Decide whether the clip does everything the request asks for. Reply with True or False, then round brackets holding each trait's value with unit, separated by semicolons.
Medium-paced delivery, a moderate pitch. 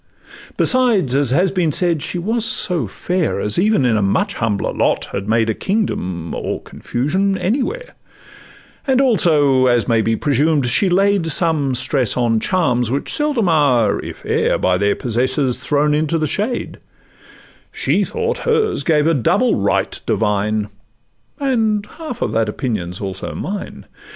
True (155 wpm; 150 Hz)